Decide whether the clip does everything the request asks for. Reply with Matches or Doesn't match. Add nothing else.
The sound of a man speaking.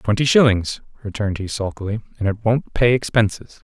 Matches